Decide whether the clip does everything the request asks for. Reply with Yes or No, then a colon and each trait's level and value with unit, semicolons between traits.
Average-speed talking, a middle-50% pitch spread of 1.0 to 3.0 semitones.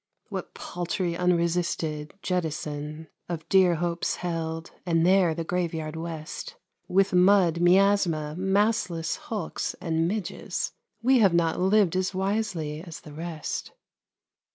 No: slow, 120 wpm; average, 2.7 semitones